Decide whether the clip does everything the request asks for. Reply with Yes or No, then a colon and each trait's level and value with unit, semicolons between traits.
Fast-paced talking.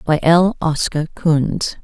No: slow, 130 wpm